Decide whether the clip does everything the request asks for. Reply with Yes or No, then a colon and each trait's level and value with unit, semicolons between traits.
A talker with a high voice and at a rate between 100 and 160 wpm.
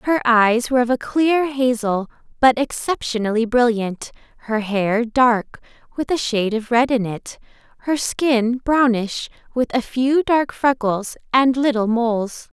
Yes: high, 240 Hz; average, 150 wpm